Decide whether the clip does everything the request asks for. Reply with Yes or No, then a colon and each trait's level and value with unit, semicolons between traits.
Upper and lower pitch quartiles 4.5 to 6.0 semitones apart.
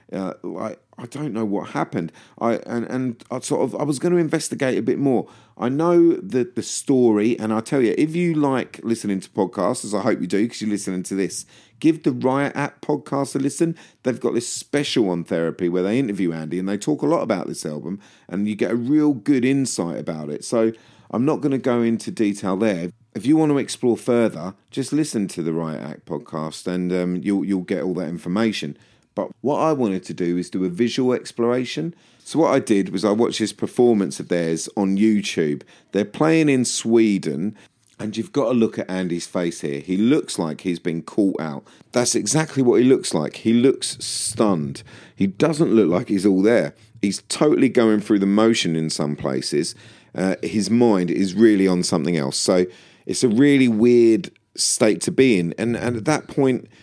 Yes: average, 5.3 semitones